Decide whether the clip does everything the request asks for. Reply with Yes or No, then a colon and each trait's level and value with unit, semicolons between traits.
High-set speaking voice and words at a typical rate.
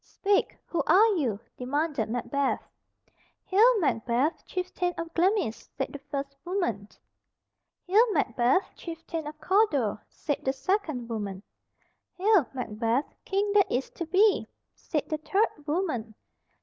No: very high, 310 Hz; slow, 125 wpm